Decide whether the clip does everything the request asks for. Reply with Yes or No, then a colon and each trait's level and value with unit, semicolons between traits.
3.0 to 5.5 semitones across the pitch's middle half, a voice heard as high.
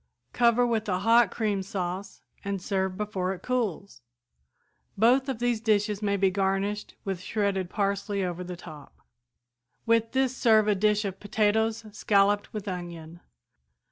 No: narrow, 2.6 semitones; high, 205 Hz